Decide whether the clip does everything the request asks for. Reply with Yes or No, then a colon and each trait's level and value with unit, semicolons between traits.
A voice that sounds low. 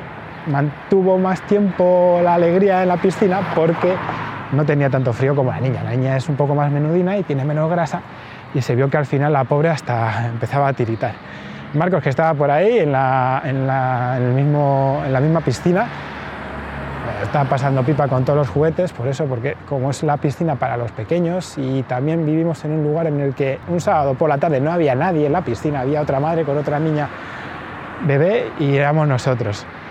No: medium, 145 Hz